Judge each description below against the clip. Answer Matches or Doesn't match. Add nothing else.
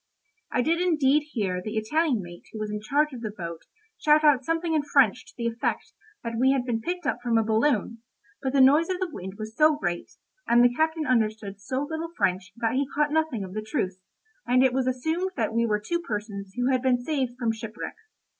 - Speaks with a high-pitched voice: Matches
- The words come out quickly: Matches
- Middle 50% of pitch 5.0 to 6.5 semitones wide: Matches